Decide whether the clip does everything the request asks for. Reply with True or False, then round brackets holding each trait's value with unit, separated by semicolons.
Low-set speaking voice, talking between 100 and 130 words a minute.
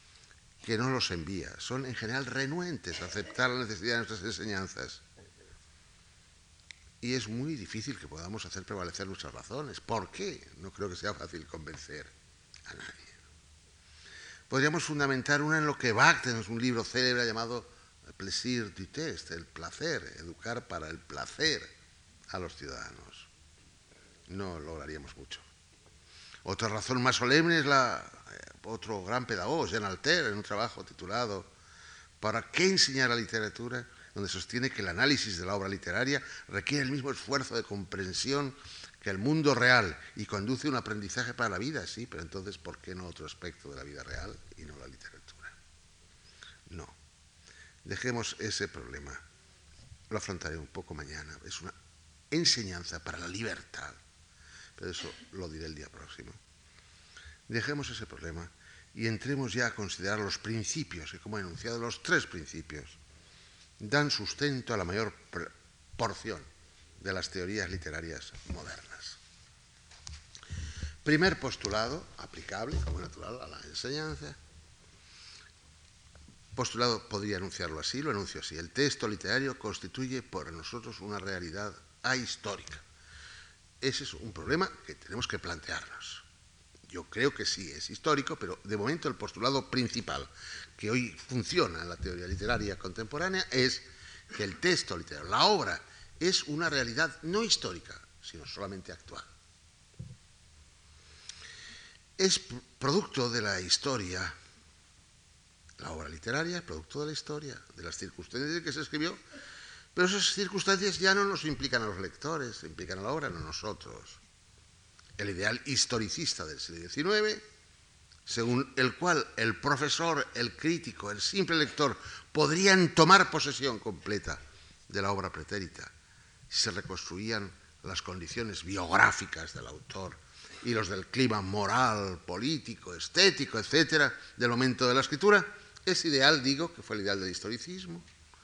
False (100 Hz; 145 wpm)